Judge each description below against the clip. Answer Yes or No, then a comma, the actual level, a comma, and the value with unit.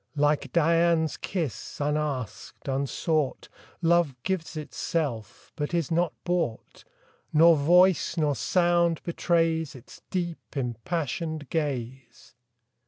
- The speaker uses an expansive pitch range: No, average, 3.4 semitones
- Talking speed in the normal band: No, slow, 100 wpm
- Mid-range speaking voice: Yes, medium, 160 Hz